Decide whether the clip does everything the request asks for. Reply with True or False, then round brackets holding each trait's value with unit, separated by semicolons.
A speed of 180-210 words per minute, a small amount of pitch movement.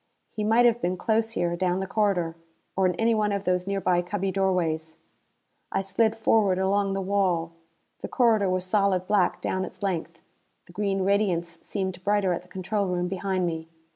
True (185 wpm; 2.3 semitones)